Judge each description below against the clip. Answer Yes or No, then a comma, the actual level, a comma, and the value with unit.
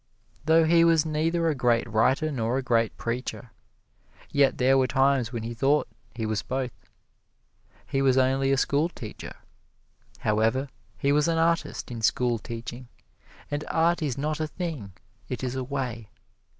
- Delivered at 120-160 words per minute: Yes, average, 155 wpm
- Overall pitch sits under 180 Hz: Yes, low, 135 Hz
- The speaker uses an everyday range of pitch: Yes, average, 4.3 semitones